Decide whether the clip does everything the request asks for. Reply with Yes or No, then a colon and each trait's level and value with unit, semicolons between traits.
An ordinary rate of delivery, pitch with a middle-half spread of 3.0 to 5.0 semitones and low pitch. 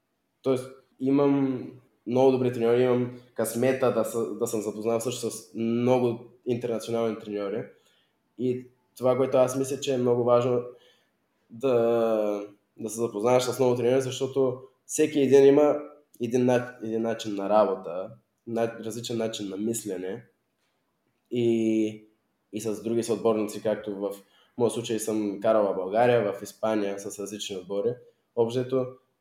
No: average, 135 wpm; narrow, 2.6 semitones; low, 120 Hz